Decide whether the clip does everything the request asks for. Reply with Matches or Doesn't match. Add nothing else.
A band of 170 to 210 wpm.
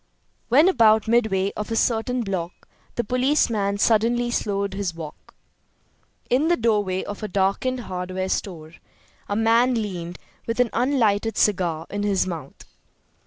Doesn't match